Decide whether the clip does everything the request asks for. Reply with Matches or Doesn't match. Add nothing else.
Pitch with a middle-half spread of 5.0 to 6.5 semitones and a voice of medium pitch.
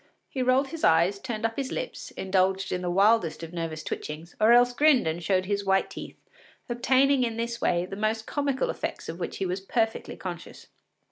Doesn't match